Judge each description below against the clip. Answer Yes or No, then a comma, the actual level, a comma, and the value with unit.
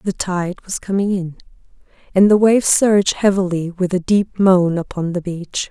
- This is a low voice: No, medium, 185 Hz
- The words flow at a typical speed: Yes, average, 180 wpm